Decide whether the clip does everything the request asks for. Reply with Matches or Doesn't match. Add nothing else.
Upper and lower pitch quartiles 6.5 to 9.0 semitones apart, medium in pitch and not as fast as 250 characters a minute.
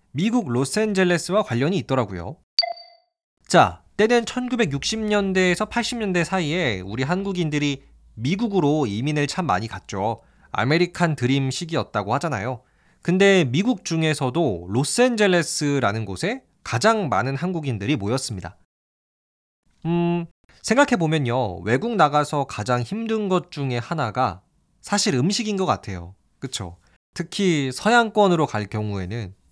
Doesn't match